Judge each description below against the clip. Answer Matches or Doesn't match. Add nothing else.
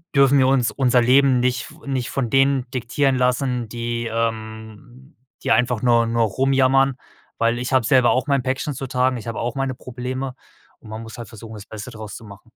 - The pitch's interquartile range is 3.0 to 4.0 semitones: Doesn't match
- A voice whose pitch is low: Matches